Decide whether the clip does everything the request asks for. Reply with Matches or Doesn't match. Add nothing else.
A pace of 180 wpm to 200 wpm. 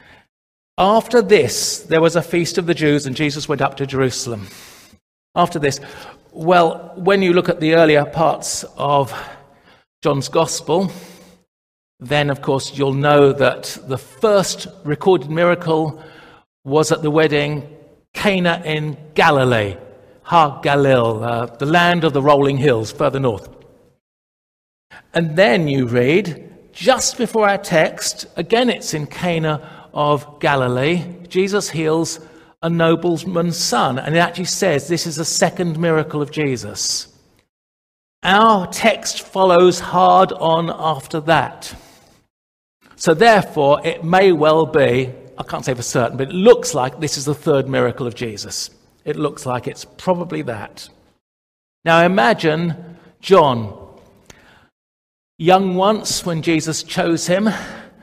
Doesn't match